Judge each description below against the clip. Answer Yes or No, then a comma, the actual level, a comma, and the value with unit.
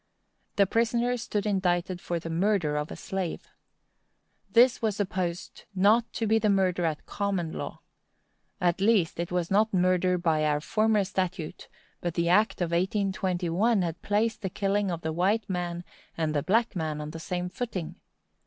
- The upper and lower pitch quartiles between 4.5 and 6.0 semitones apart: No, average, 3.4 semitones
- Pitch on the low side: No, medium, 185 Hz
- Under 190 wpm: Yes, average, 165 wpm